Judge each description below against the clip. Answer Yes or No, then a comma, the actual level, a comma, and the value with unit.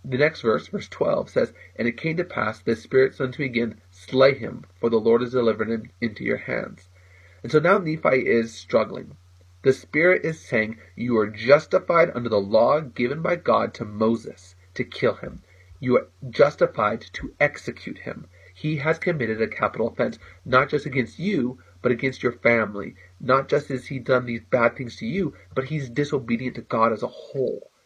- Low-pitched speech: Yes, low, 120 Hz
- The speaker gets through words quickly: No, average, 190 wpm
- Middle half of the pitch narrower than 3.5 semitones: No, average, 4.0 semitones